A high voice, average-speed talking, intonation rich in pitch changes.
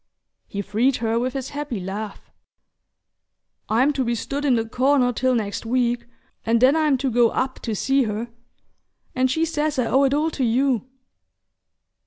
No: very high, 255 Hz; average, 175 wpm; average, 3.2 semitones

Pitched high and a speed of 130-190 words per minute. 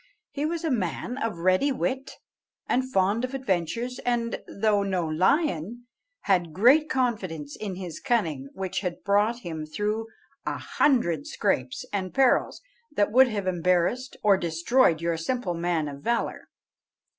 Yes: high, 200 Hz; average, 145 wpm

